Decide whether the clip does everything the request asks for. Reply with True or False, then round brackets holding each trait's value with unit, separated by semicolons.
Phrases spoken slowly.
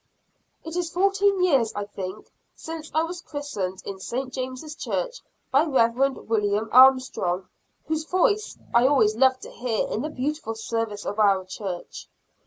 False (155 wpm)